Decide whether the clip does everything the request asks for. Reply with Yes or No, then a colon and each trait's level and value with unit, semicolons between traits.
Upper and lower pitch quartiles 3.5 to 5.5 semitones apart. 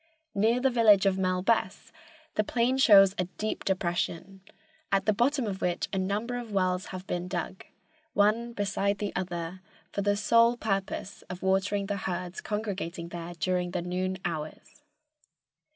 No: average, 2.7 semitones